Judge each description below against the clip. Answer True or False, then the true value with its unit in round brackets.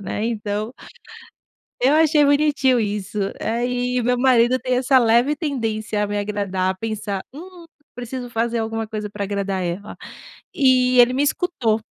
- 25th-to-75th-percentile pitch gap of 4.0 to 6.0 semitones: False (3.6 semitones)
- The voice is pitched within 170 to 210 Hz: False (235 Hz)